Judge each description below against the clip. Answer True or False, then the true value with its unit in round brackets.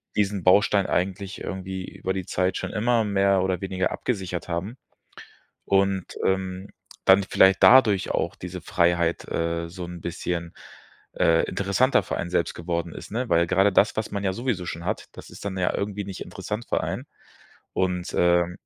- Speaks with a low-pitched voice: True (95 Hz)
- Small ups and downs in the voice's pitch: True (2.3 semitones)